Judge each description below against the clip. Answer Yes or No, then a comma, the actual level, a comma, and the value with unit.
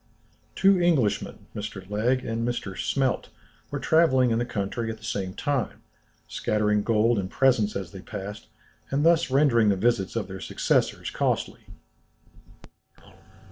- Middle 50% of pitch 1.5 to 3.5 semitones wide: No, average, 4.2 semitones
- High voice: No, low, 115 Hz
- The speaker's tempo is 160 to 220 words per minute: No, average, 140 wpm